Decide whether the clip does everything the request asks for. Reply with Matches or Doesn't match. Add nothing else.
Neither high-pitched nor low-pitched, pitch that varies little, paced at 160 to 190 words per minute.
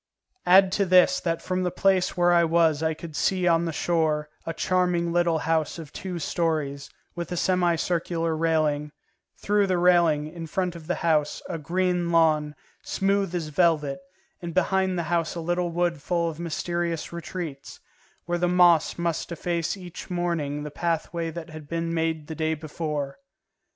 Matches